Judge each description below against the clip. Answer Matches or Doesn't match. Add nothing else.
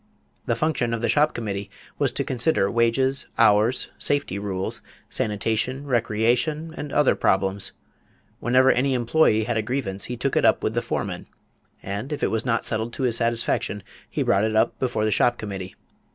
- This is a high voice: Doesn't match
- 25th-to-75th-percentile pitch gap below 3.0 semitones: Doesn't match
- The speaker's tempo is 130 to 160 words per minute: Doesn't match